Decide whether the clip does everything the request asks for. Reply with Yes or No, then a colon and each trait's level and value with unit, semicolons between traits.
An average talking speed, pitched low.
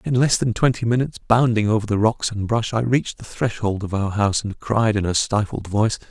No: fast, 235 wpm; low, 110 Hz